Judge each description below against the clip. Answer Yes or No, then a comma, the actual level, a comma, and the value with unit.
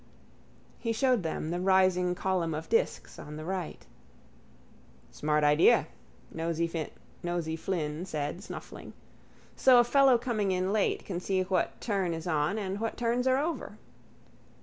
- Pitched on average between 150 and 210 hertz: Yes, medium, 185 Hz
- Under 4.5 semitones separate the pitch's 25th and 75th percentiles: No, average, 5.0 semitones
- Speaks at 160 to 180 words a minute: No, average, 140 wpm